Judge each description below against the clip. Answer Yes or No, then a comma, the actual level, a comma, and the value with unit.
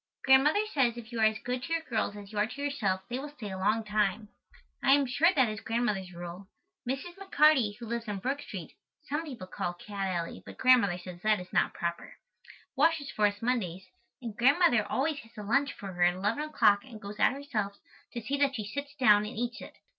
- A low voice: No, high, 225 Hz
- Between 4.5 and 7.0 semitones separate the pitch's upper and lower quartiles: Yes, average, 5.3 semitones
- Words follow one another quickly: Yes, fast, 230 wpm